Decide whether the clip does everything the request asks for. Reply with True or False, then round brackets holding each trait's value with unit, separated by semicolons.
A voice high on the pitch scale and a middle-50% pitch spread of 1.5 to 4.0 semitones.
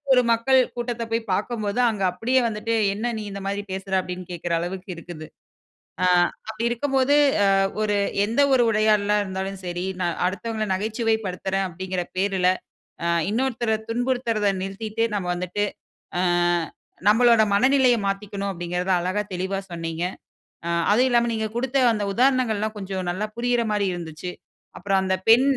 True (210 Hz; 3.7 semitones)